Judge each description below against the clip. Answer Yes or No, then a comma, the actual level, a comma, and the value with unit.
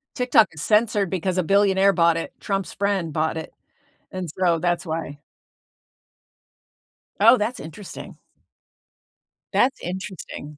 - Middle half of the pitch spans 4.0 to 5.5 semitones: No, average, 3.5 semitones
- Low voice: No, medium, 185 Hz